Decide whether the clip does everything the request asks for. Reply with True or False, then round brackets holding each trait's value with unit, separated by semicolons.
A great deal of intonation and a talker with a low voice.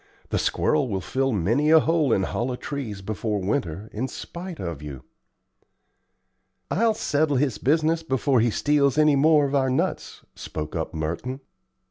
True (6.6 semitones; 130 Hz)